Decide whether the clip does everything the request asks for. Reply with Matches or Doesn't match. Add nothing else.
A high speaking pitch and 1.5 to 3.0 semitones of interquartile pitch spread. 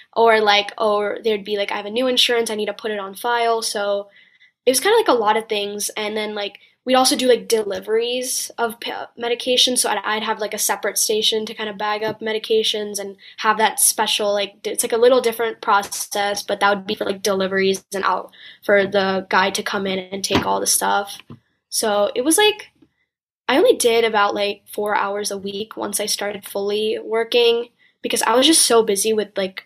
Matches